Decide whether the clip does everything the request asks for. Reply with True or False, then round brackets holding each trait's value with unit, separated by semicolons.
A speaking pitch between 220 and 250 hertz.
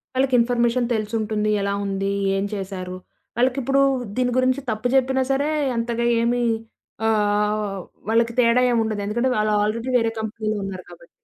True (225 Hz)